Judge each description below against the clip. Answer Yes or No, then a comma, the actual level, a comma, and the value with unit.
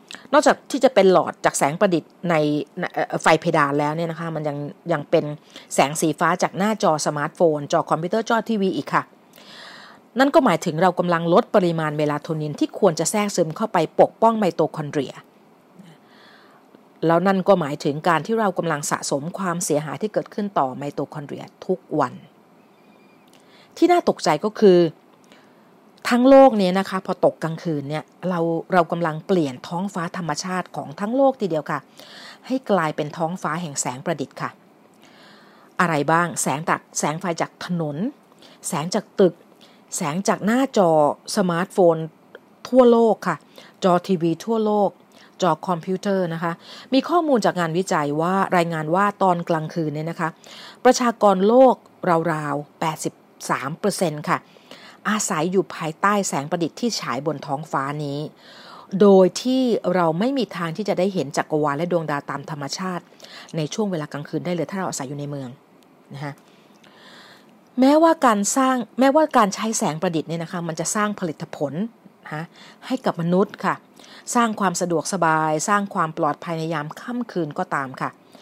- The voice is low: No, medium, 180 Hz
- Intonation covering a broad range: No, average, 4.7 semitones